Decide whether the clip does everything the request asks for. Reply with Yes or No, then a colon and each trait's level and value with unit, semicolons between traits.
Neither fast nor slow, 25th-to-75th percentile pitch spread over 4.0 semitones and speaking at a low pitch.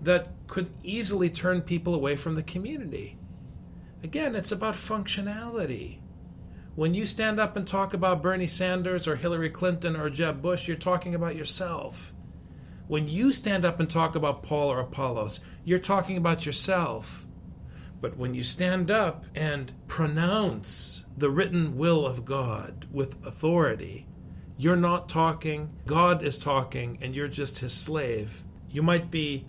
No: average, 150 wpm; average, 4.8 semitones; medium, 165 Hz